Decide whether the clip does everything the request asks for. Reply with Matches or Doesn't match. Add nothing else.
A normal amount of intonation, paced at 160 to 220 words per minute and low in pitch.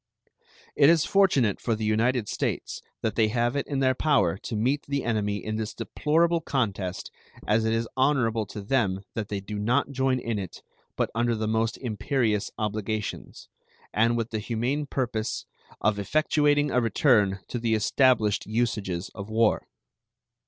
Matches